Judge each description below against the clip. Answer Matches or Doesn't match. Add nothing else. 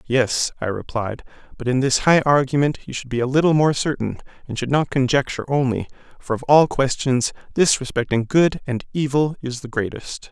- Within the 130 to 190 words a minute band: Matches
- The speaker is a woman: Doesn't match